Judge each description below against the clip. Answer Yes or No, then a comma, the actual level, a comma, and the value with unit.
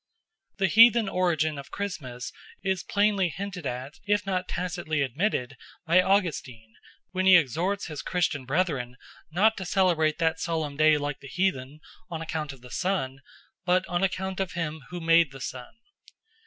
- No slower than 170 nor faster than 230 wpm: No, average, 160 wpm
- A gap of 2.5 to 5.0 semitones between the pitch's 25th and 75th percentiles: Yes, average, 4.6 semitones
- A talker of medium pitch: Yes, medium, 170 Hz